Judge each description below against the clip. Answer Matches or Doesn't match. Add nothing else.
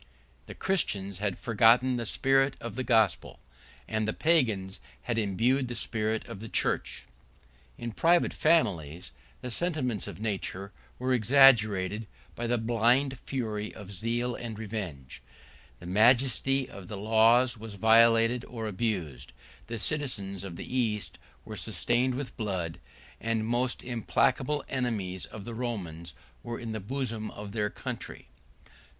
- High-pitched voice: Doesn't match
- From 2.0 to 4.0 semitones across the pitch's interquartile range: Matches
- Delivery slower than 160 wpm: Matches